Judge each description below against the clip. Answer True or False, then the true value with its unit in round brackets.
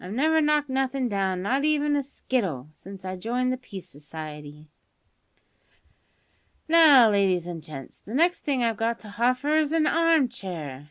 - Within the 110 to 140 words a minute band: False (165 wpm)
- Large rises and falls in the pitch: True (7.9 semitones)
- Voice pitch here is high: True (235 Hz)